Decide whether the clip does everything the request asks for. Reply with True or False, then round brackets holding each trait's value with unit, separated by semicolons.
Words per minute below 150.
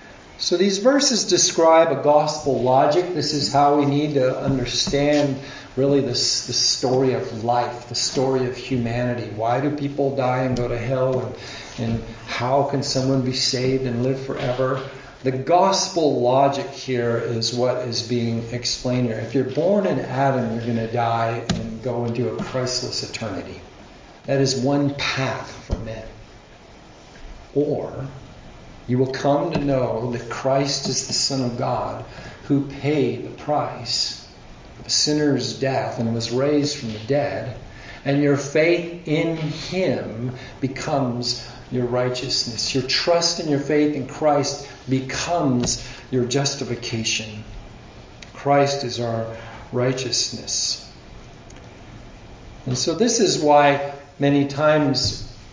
True (140 wpm)